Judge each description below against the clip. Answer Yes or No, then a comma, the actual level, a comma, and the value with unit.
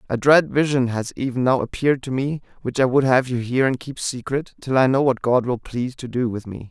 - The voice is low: Yes, low, 130 Hz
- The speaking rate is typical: No, fast, 260 wpm